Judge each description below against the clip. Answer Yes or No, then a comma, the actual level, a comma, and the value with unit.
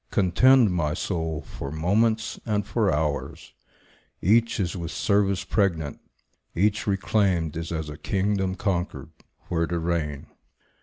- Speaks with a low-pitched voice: Yes, very low, 90 Hz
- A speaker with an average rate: No, slow, 130 wpm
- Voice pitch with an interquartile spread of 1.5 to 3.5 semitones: No, average, 4.1 semitones